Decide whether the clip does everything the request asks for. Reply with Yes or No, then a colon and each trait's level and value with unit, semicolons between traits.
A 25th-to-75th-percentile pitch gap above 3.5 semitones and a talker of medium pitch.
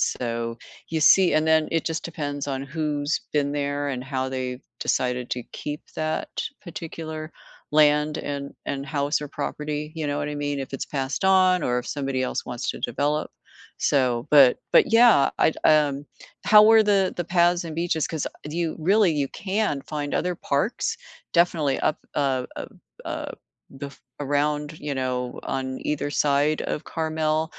No: narrow, 2.5 semitones; medium, 150 Hz